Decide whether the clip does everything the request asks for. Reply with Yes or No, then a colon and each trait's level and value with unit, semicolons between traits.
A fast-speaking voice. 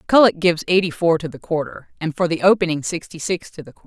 Yes: fast, 250 wpm